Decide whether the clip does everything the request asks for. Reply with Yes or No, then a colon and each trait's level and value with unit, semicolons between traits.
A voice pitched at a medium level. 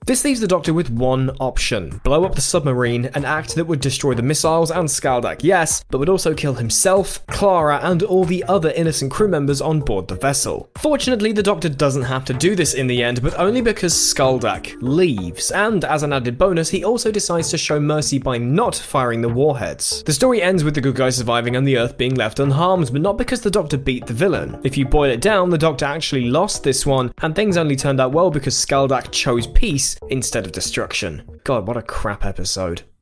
Yes: medium, 145 Hz